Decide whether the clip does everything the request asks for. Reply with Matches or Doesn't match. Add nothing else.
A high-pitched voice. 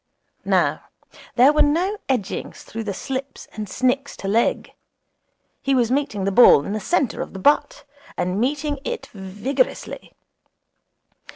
Matches